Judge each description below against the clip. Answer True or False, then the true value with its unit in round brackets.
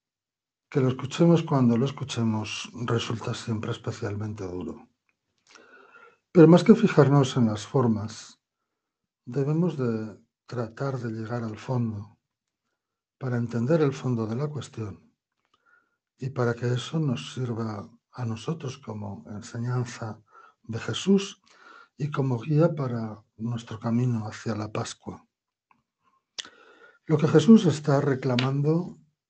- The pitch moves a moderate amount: True (5.0 semitones)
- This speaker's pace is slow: True (115 wpm)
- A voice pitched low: True (125 Hz)